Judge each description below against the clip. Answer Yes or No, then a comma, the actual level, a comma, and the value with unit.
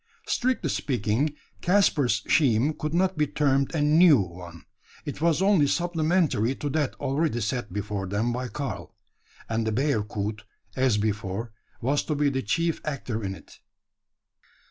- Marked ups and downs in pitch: Yes, wide, 6.1 semitones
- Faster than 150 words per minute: No, average, 145 wpm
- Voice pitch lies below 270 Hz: Yes, low, 135 Hz